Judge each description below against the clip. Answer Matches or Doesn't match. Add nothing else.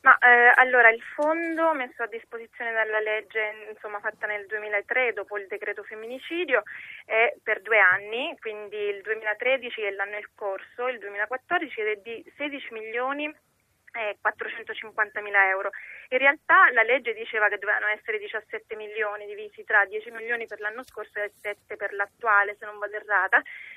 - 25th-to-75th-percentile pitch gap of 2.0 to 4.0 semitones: Matches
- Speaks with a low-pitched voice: Doesn't match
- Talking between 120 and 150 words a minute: Doesn't match